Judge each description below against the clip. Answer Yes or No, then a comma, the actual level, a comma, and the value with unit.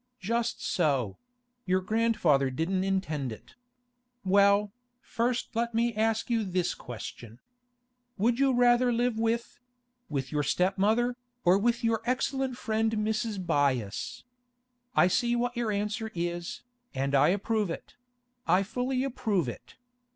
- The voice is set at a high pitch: Yes, high, 215 Hz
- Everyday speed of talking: No, slow, 130 wpm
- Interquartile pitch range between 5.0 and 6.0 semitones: Yes, wide, 5.4 semitones